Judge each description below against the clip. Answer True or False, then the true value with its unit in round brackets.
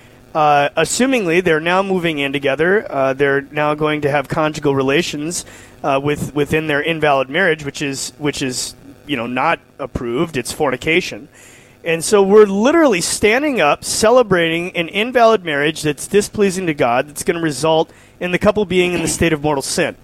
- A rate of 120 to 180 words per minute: True (175 wpm)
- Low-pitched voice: False (155 Hz)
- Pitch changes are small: False (3.9 semitones)